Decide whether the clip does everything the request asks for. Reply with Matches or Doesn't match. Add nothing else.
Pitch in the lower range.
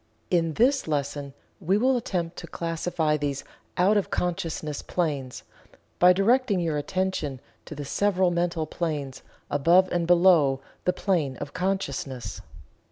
Doesn't match